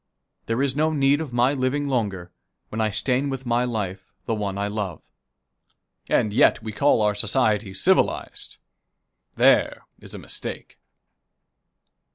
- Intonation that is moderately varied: Yes, average, 4.5 semitones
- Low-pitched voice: Yes, low, 115 Hz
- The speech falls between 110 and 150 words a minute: Yes, average, 145 wpm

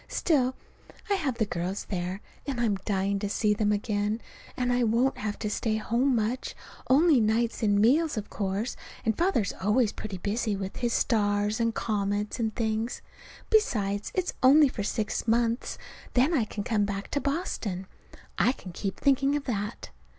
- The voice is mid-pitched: No, high, 220 Hz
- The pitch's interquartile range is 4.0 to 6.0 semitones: No, average, 3.6 semitones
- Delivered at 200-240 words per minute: No, average, 170 wpm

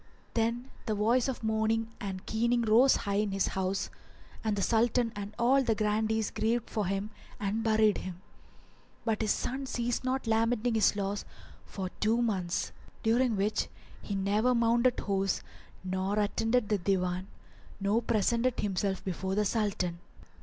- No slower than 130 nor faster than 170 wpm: Yes, average, 155 wpm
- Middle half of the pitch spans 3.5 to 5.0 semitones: No, average, 2.8 semitones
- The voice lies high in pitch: Yes, high, 215 Hz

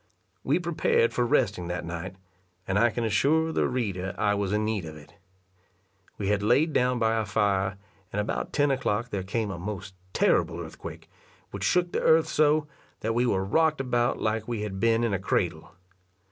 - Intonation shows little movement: No, average, 4.4 semitones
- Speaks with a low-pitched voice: Yes, low, 110 Hz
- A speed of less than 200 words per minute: Yes, average, 190 wpm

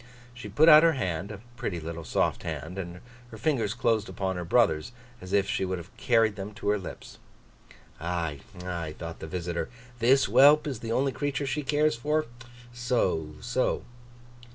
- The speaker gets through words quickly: No, average, 175 wpm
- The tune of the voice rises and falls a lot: Yes, wide, 6.4 semitones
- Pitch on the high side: No, low, 105 Hz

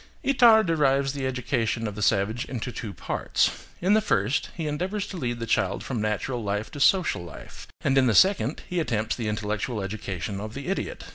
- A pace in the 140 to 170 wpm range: No, average, 200 wpm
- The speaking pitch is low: Yes, low, 120 Hz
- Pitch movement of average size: No, wide, 6.6 semitones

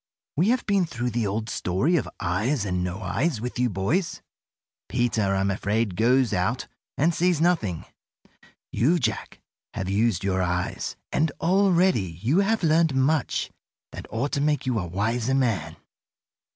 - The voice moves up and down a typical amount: No, wide, 8.1 semitones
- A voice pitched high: No, low, 120 Hz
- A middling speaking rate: Yes, average, 155 wpm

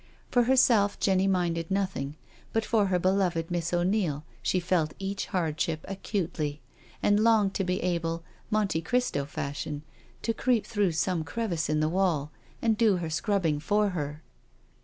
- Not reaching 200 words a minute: Yes, average, 155 wpm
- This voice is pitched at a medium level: Yes, medium, 180 Hz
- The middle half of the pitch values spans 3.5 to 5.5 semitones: Yes, average, 4.1 semitones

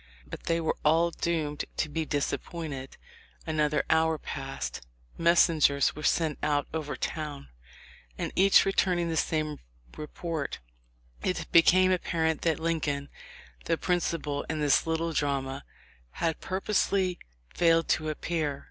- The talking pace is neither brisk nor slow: No, slow, 125 wpm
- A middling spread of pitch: No, narrow, 2.2 semitones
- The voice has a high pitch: No, medium, 160 Hz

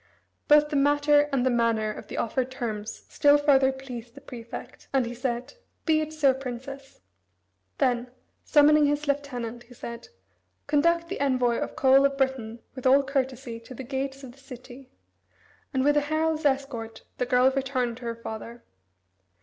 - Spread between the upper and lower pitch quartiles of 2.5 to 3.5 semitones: Yes, average, 2.9 semitones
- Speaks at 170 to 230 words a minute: Yes, average, 175 wpm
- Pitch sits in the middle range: No, very high, 265 Hz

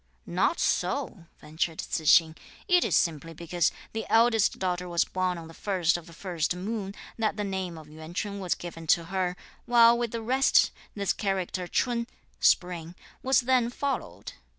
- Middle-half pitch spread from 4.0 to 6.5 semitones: Yes, average, 5.0 semitones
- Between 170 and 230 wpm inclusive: Yes, average, 175 wpm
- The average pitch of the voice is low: No, medium, 185 Hz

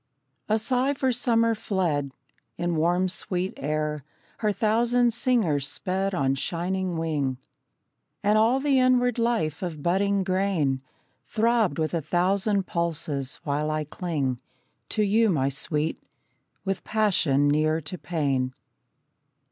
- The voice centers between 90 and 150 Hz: No, medium, 180 Hz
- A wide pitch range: Yes, wide, 6.0 semitones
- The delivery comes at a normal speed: No, slow, 125 wpm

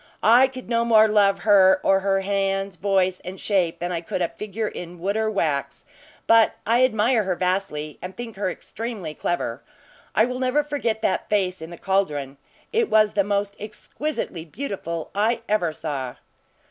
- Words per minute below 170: No, average, 175 wpm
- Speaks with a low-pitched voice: No, high, 195 Hz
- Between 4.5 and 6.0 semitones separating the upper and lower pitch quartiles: No, average, 3.7 semitones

